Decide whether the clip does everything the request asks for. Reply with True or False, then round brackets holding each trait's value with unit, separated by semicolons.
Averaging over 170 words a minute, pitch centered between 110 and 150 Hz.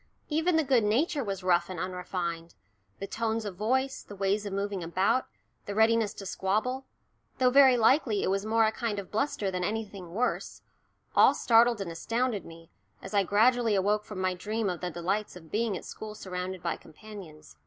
False (190 wpm; 205 Hz)